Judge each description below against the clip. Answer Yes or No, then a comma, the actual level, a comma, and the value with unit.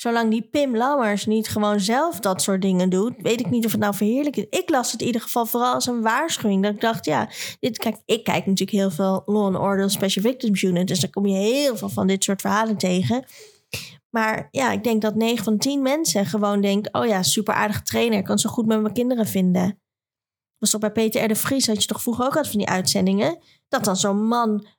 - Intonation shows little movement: No, average, 3.2 semitones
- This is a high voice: Yes, high, 215 Hz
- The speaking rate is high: Yes, fast, 245 wpm